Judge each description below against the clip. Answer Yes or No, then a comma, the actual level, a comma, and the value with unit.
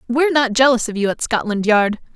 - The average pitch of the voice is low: No, high, 235 Hz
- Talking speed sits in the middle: No, fast, 225 wpm